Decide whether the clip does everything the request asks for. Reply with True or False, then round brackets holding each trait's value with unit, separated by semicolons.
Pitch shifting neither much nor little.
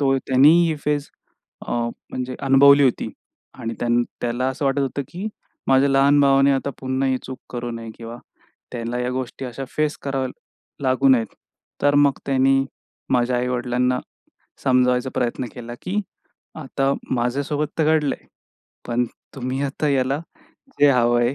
False (2.1 semitones)